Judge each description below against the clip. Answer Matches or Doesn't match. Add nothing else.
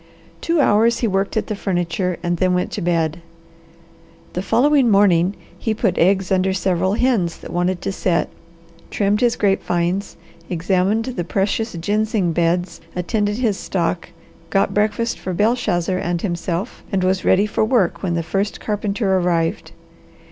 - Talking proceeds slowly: Doesn't match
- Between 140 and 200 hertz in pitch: Matches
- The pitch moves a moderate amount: Matches